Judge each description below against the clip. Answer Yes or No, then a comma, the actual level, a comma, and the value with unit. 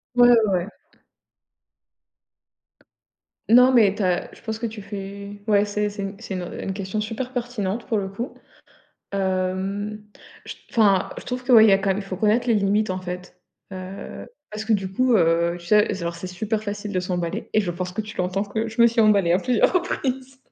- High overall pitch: Yes, high, 205 Hz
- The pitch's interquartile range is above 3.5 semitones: No, average, 2.9 semitones